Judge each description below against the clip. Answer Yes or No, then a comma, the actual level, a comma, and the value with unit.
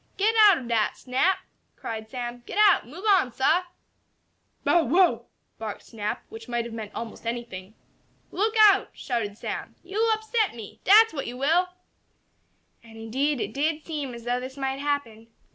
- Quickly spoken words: No, average, 165 wpm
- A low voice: No, very high, 260 Hz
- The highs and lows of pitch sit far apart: Yes, wide, 7.5 semitones